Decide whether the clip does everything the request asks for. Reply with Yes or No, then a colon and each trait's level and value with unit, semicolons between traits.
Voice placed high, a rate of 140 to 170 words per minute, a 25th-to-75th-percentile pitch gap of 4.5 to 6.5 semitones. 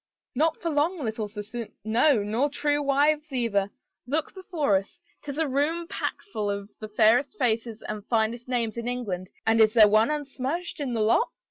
No: high, 245 Hz; average, 180 wpm; average, 5.2 semitones